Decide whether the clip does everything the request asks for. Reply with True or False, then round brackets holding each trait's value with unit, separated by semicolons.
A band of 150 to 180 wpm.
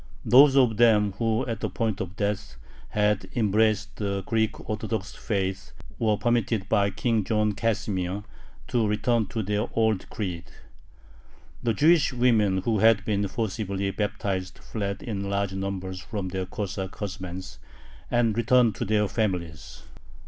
False (140 wpm)